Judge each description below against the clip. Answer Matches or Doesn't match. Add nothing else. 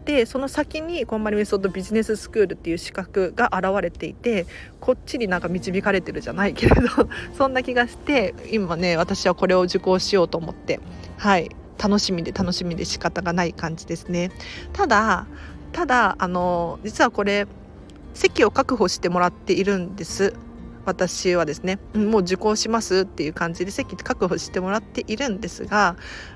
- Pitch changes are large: Doesn't match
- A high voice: Matches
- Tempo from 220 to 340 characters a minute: Doesn't match